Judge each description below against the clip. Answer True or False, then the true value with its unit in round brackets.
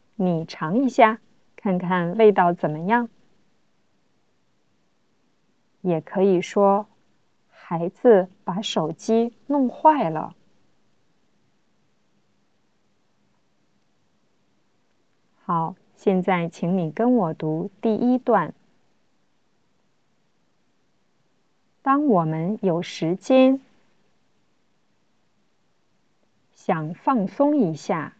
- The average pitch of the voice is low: False (200 Hz)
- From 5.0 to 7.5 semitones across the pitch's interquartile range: True (5.4 semitones)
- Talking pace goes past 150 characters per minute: False (95 characters per minute)